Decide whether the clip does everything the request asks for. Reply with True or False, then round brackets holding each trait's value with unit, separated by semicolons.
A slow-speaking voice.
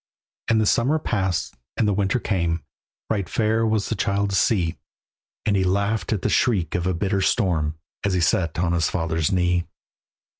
False (185 wpm)